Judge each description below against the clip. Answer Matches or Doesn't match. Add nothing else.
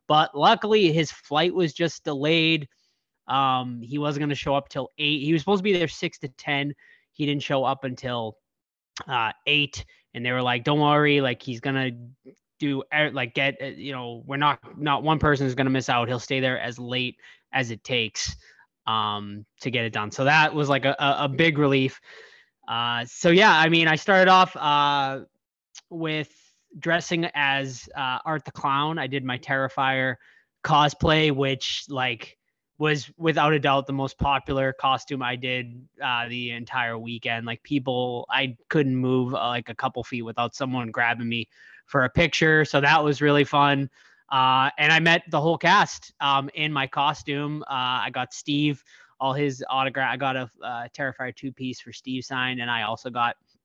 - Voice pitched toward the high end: Doesn't match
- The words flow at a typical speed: Matches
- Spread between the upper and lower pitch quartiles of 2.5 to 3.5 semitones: Matches